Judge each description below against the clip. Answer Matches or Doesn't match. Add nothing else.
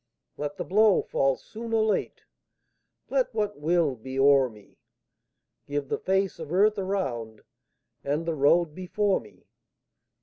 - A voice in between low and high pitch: Matches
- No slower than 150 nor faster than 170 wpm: Doesn't match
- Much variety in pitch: Matches